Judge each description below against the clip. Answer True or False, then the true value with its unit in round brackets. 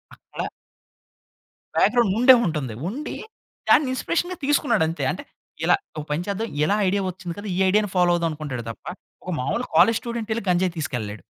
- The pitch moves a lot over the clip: True (6.7 semitones)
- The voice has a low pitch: False (185 Hz)